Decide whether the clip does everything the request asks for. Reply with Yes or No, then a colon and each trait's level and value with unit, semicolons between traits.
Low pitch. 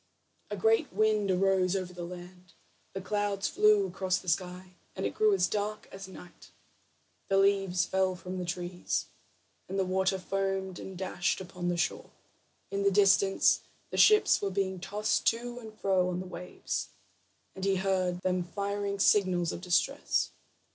No: high, 190 Hz